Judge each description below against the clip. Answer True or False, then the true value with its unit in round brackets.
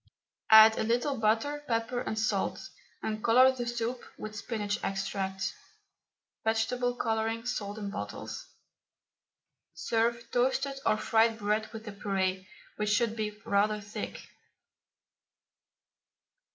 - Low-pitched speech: False (220 Hz)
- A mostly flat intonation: True (2.1 semitones)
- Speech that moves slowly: True (115 wpm)